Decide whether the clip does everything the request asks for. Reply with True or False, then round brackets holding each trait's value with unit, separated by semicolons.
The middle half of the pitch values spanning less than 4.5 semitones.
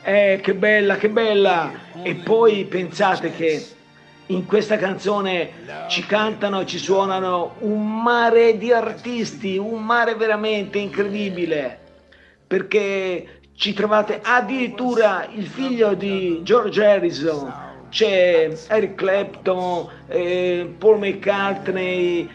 True (2.9 semitones)